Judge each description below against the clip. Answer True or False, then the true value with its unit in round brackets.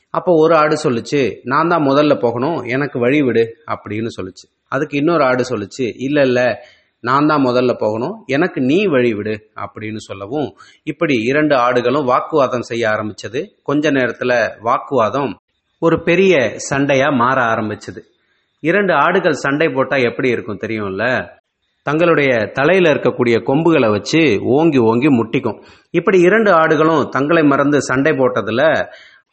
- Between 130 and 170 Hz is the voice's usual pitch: True (135 Hz)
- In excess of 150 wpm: False (135 wpm)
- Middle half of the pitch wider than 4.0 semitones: True (4.7 semitones)